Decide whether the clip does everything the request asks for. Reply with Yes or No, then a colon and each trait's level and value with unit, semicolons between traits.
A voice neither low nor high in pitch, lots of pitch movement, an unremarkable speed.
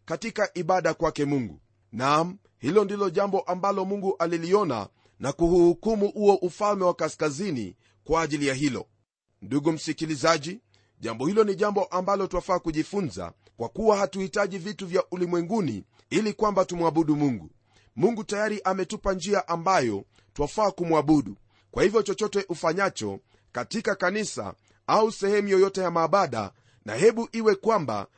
Yes: medium, 175 Hz; wide, 5.8 semitones; average, 130 wpm